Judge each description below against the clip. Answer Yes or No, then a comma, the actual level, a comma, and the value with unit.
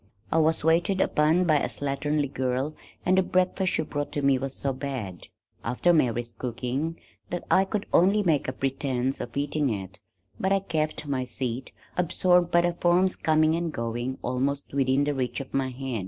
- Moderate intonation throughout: Yes, average, 4.6 semitones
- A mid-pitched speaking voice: Yes, medium, 145 Hz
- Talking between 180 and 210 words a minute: Yes, average, 185 wpm